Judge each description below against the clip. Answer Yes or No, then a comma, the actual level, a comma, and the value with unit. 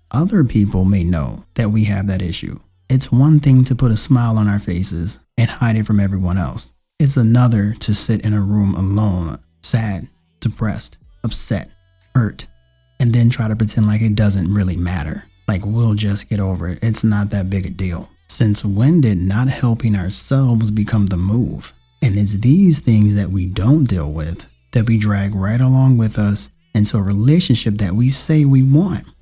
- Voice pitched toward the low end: Yes, low, 105 Hz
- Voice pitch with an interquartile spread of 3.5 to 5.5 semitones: Yes, average, 3.8 semitones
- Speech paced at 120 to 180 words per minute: No, average, 190 wpm